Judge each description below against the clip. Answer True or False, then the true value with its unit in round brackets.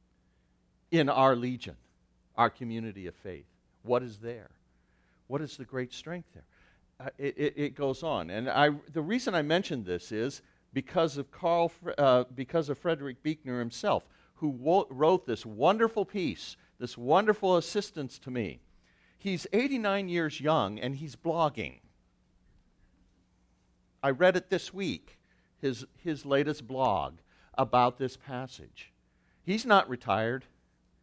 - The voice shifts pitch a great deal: True (7.4 semitones)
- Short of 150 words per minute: True (140 wpm)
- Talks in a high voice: False (135 Hz)